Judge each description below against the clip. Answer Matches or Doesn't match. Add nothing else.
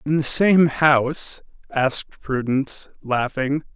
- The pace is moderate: Doesn't match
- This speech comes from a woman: Doesn't match